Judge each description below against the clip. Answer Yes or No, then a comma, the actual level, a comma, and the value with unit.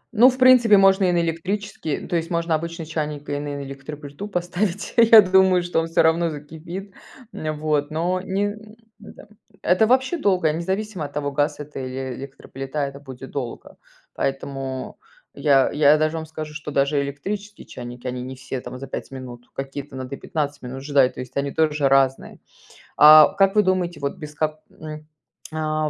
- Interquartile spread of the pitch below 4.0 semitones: No, average, 4.5 semitones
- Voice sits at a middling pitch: Yes, medium, 155 Hz